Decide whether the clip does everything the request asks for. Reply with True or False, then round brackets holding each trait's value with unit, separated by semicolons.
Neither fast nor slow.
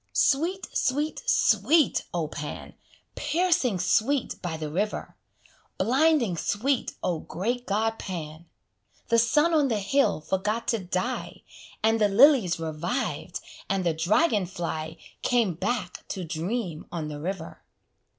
False (130 wpm)